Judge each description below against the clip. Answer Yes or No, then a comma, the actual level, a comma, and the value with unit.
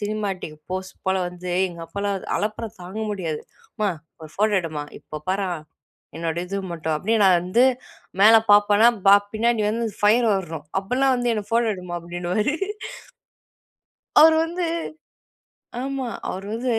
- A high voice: Yes, high, 205 Hz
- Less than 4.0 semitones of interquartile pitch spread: No, average, 4.3 semitones